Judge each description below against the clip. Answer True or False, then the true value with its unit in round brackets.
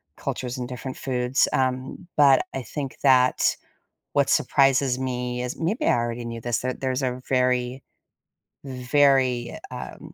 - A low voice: True (130 Hz)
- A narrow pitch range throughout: True (1.3 semitones)